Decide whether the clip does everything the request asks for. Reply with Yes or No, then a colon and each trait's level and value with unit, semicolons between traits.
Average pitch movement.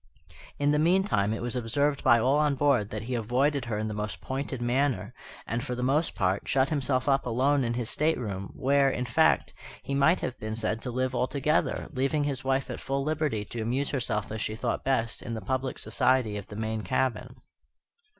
Yes: average, 3.8 semitones